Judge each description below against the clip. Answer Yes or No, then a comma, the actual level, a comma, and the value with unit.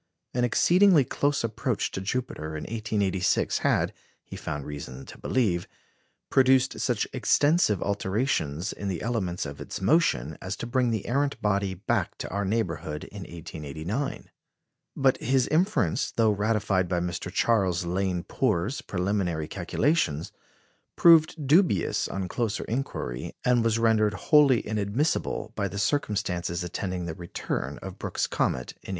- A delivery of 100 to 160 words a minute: Yes, average, 145 wpm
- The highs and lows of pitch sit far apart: Yes, wide, 6.2 semitones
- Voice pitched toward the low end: Yes, low, 105 Hz